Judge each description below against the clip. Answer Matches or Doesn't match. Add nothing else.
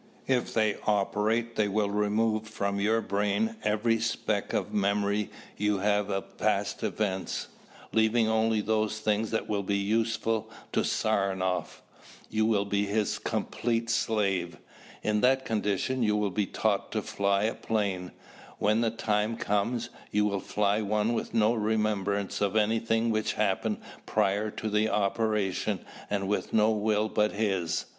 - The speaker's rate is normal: Matches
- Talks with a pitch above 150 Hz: Doesn't match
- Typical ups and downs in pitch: Doesn't match